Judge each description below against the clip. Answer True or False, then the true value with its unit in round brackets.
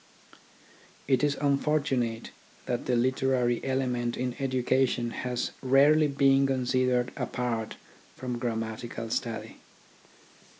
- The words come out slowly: True (95 wpm)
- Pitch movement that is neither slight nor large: False (2.1 semitones)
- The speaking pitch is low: True (125 Hz)